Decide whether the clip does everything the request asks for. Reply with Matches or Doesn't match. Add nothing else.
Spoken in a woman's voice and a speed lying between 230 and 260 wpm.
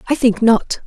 Doesn't match